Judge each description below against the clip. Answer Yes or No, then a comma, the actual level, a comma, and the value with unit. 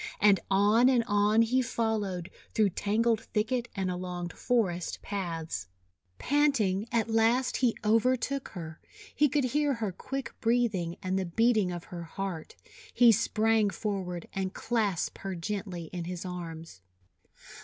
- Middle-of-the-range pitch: No, high, 205 Hz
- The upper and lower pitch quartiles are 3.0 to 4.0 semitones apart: No, average, 4.4 semitones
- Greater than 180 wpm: No, average, 145 wpm